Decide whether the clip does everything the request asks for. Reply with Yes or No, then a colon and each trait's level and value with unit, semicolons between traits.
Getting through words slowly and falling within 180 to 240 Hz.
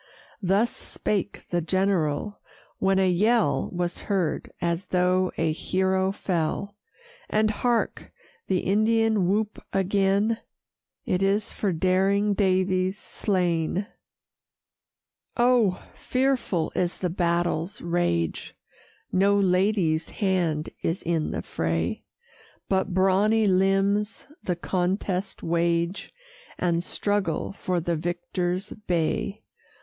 Yes: slow, 105 wpm; high, 190 Hz